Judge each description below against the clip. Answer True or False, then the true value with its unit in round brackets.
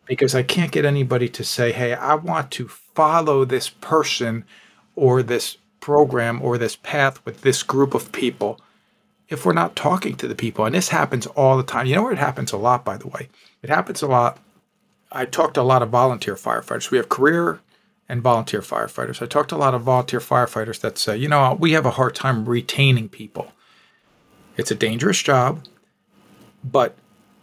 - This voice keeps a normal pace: True (195 wpm)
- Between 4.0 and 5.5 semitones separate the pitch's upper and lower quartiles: False (3.1 semitones)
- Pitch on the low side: True (130 Hz)